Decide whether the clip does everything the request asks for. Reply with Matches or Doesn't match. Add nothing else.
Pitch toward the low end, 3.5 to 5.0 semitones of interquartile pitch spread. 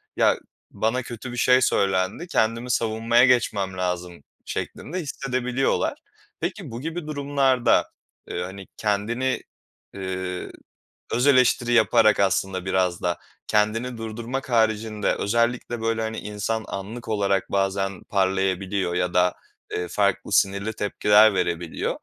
Matches